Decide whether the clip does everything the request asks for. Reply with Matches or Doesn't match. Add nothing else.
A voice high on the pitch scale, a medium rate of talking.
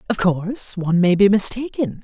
Matches